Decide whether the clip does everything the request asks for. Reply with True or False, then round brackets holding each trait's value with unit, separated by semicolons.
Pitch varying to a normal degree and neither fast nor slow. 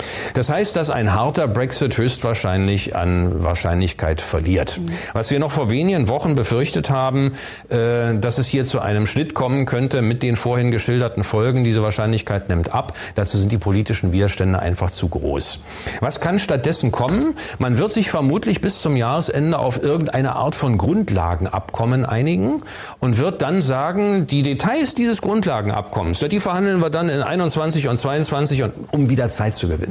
False (5.9 semitones; 170 wpm)